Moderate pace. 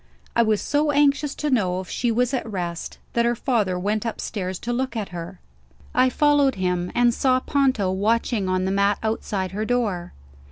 Yes: average, 190 wpm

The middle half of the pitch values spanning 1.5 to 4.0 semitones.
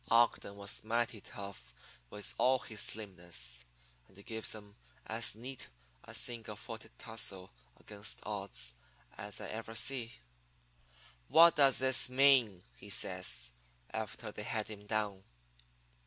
Yes: average, 2.9 semitones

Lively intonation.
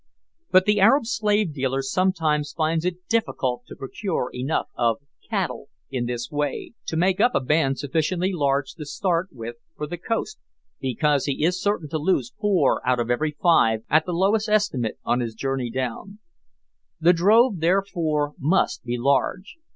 Yes: wide, 5.8 semitones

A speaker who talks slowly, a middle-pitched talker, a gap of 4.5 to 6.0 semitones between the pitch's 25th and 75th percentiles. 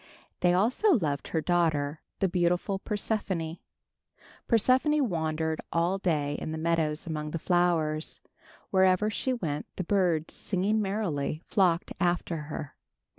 No: slow, 125 wpm; medium, 175 Hz; average, 3.7 semitones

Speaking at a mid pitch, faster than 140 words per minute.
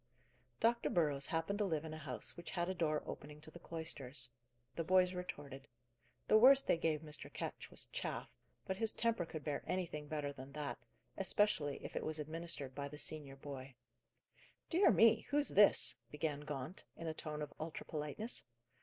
Yes: medium, 155 Hz; average, 180 wpm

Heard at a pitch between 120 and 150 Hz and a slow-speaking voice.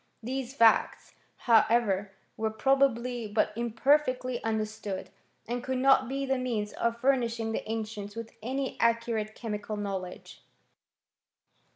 No: high, 230 Hz; slow, 125 wpm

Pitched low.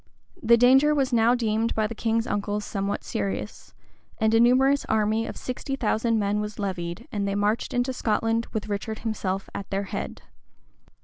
No: high, 220 Hz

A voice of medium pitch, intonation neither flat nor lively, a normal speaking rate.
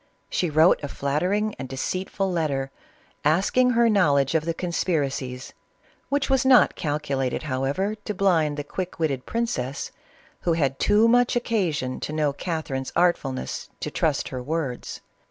No: medium, 160 Hz; wide, 6.1 semitones; average, 150 wpm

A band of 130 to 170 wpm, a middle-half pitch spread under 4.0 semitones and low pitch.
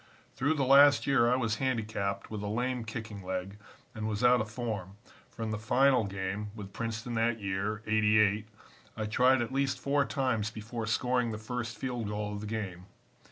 No: average, 190 wpm; average, 2.9 semitones; low, 110 Hz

